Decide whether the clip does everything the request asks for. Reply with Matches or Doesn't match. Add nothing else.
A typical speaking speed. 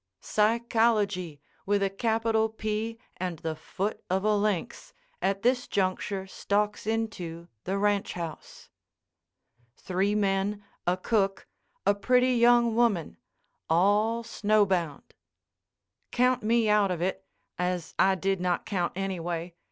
Doesn't match